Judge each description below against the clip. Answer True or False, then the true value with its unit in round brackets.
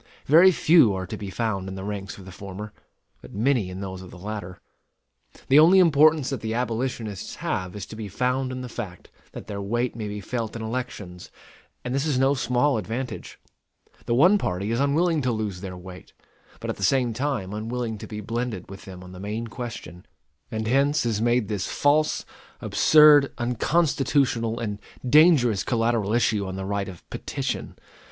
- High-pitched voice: False (115 Hz)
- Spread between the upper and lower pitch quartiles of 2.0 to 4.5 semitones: False (4.9 semitones)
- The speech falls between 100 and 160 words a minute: False (190 wpm)